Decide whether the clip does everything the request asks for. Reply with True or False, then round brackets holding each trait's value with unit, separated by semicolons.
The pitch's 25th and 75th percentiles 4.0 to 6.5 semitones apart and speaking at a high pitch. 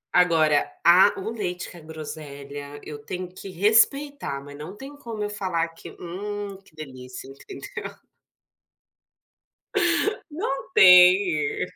False (5.3 semitones; 180 Hz)